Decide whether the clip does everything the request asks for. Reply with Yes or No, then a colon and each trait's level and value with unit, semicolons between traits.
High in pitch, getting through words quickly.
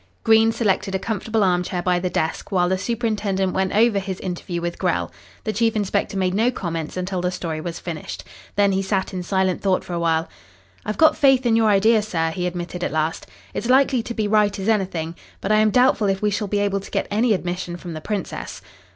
Yes: high, 195 Hz; fast, 230 wpm